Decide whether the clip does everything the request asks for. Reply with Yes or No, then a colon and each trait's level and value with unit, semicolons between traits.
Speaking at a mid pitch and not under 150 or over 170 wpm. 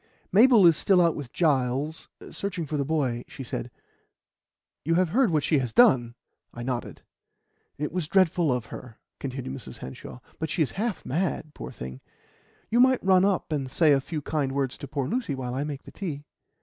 No: medium, 150 Hz; average, 195 wpm